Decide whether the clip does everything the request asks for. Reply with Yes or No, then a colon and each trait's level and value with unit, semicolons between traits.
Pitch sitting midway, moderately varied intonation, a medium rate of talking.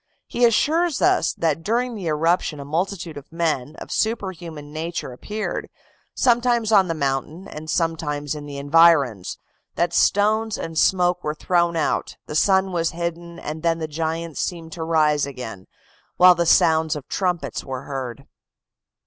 Yes: medium, 165 Hz; average, 3.3 semitones; average, 155 wpm